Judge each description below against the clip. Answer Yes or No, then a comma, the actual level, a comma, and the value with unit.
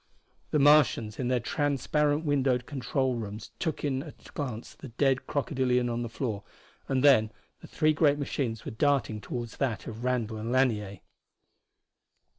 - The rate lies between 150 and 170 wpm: Yes, average, 160 wpm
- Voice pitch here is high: No, low, 130 Hz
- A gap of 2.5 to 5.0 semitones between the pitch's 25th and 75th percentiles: Yes, average, 3.8 semitones